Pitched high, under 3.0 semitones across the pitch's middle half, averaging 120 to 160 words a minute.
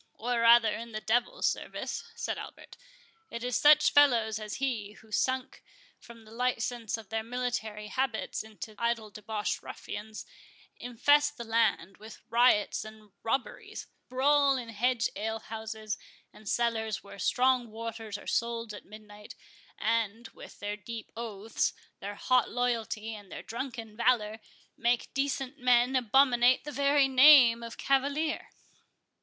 Yes: high, 230 Hz; narrow, 2.6 semitones; average, 140 wpm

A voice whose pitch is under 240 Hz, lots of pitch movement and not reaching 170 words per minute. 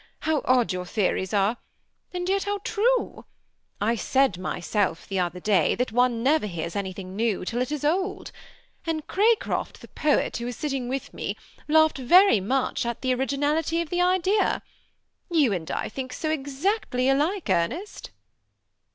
No: very high, 265 Hz; wide, 7.4 semitones; average, 160 wpm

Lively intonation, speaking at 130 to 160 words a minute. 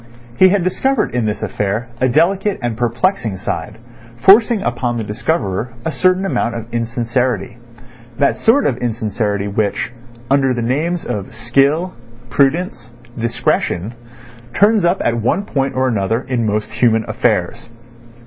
Yes: wide, 6.0 semitones; average, 140 wpm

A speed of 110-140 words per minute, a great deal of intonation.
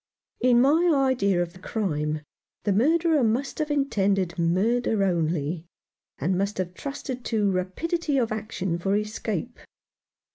Yes: slow, 135 wpm; wide, 6.2 semitones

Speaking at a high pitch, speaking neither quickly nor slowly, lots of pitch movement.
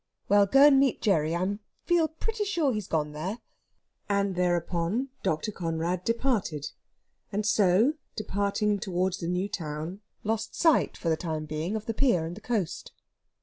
No: high, 195 Hz; average, 160 wpm; average, 4.7 semitones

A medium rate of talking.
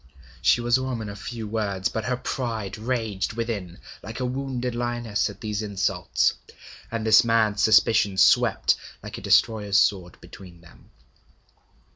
Yes: average, 150 wpm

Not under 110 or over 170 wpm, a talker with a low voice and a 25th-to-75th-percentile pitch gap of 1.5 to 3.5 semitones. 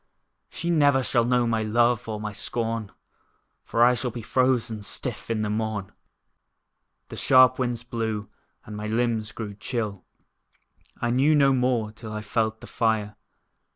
Yes: average, 155 wpm; low, 115 Hz; narrow, 2.5 semitones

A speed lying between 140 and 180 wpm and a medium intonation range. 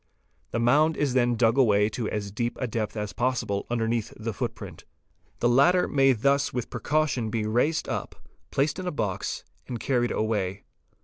Yes: average, 175 wpm; average, 3.9 semitones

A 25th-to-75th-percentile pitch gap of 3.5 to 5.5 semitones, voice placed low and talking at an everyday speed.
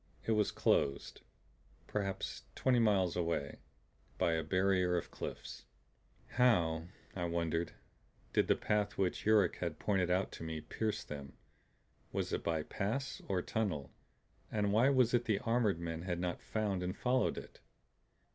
Yes: average, 4.3 semitones; very low, 95 Hz; average, 150 wpm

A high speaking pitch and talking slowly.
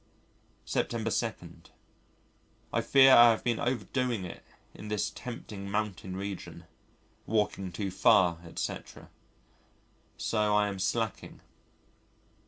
No: low, 105 Hz; slow, 105 wpm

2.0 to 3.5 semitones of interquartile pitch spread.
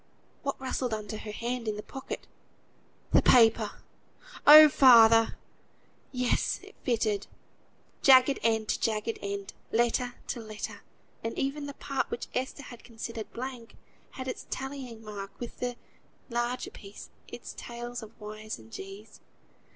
Yes: average, 2.9 semitones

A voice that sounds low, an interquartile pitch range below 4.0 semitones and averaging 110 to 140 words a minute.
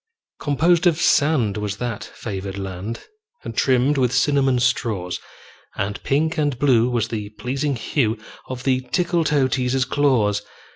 No: low, 125 Hz; average, 4.6 semitones; slow, 135 wpm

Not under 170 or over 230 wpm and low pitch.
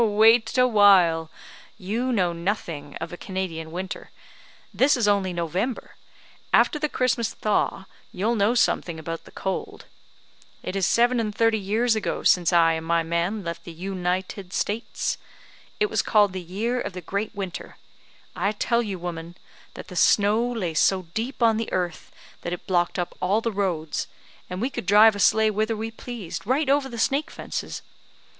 No: average, 180 wpm; high, 200 Hz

